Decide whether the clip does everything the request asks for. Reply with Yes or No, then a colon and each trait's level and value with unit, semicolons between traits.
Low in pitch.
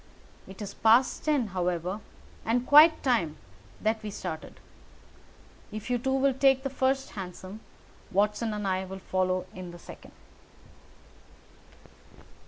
No: high, 210 Hz